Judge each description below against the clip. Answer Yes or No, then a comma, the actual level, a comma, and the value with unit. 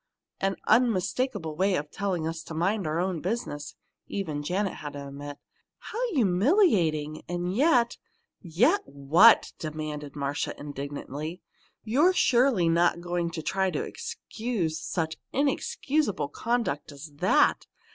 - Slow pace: Yes, slow, 130 wpm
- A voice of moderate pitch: Yes, medium, 175 Hz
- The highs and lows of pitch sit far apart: Yes, wide, 6.9 semitones